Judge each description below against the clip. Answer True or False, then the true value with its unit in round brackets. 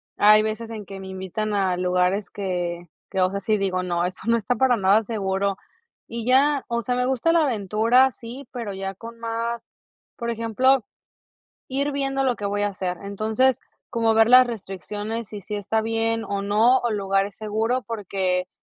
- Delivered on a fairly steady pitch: False (3.2 semitones)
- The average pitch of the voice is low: False (215 Hz)